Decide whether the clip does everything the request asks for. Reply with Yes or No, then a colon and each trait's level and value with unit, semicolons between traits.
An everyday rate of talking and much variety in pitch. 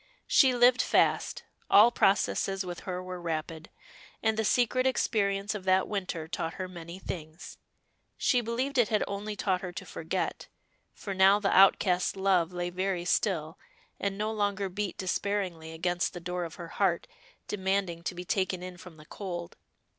No: average, 170 wpm; narrow, 2.6 semitones